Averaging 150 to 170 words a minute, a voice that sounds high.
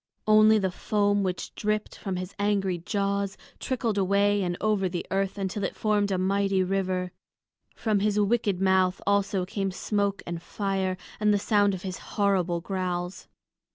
Yes: average, 160 wpm; high, 195 Hz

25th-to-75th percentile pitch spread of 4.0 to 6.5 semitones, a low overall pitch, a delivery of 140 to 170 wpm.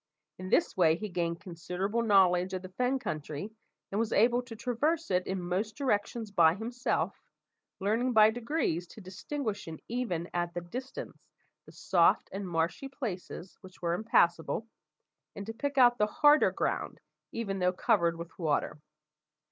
No: average, 5.0 semitones; high, 200 Hz; average, 155 wpm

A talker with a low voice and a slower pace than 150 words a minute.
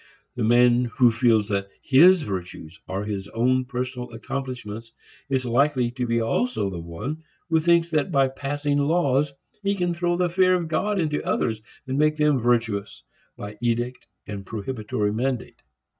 No: low, 125 Hz; average, 160 wpm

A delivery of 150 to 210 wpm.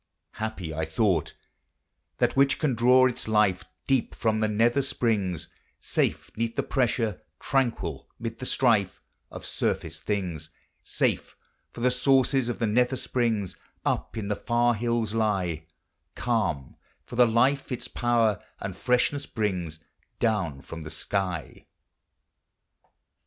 No: average, 140 wpm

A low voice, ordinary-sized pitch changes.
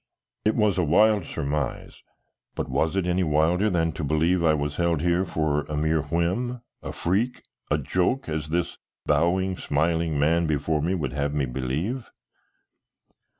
Yes: very low, 80 Hz; average, 3.4 semitones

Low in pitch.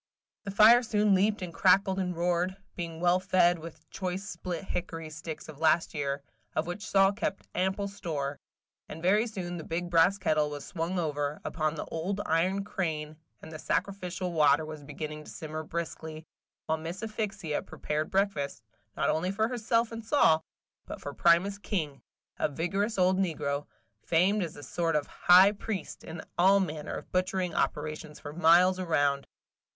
No: medium, 175 Hz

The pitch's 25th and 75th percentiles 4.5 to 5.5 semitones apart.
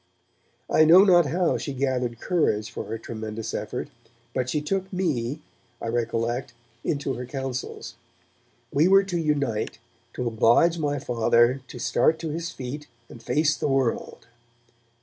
Yes: average, 5.2 semitones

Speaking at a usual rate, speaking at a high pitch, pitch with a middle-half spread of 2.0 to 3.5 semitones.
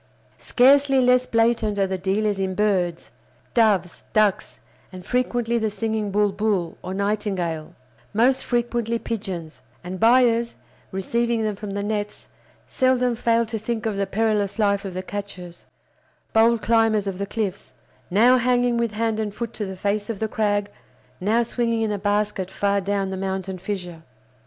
Yes: average, 155 wpm; high, 210 Hz; average, 2.9 semitones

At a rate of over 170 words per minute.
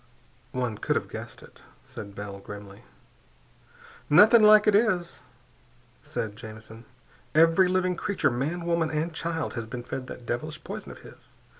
No: average, 150 wpm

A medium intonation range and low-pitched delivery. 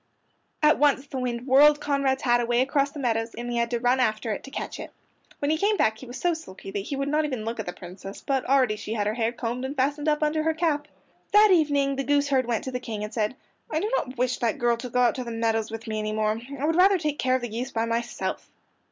No: average, 4.0 semitones; very high, 255 Hz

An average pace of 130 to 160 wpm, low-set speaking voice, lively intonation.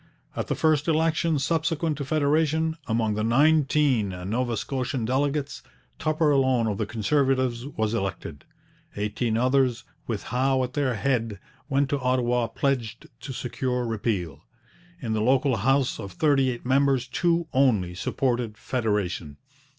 No: average, 140 wpm; low, 130 Hz; average, 4.0 semitones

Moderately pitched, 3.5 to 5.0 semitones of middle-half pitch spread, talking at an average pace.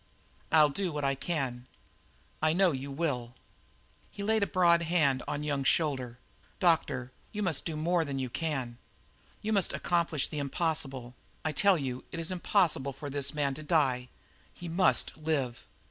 Yes: medium, 150 Hz; average, 4.0 semitones; average, 165 wpm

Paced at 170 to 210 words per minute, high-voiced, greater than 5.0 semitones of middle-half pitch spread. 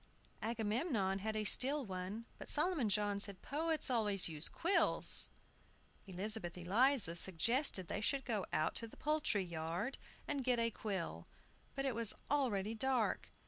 No: average, 150 wpm; high, 220 Hz; wide, 5.5 semitones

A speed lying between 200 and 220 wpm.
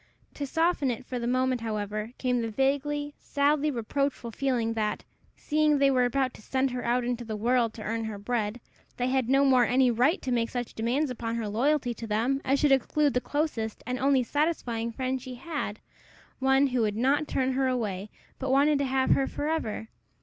Yes: fast, 205 wpm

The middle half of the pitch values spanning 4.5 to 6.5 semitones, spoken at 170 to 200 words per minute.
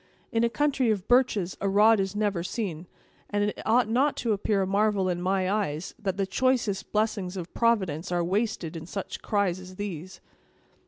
No: average, 3.0 semitones; average, 190 wpm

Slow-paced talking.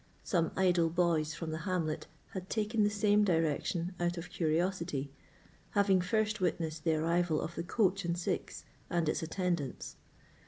No: average, 155 wpm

